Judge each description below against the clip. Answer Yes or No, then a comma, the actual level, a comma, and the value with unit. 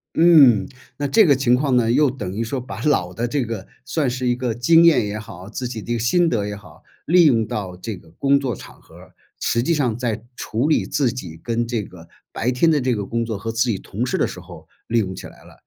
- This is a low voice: Yes, low, 120 Hz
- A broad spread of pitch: No, average, 4.3 semitones